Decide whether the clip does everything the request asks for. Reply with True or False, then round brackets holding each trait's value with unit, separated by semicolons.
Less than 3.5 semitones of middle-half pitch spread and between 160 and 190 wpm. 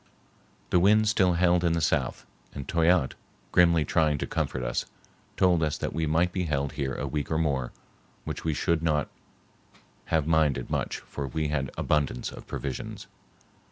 True (3.0 semitones; 170 wpm)